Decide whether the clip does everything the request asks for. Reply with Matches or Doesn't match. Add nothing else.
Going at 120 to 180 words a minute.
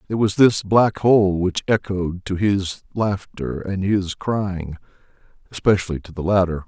Matches